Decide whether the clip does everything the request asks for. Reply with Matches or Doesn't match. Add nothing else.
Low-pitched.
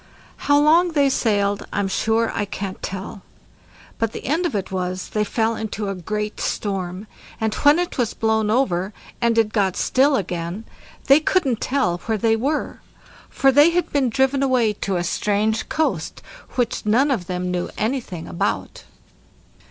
Doesn't match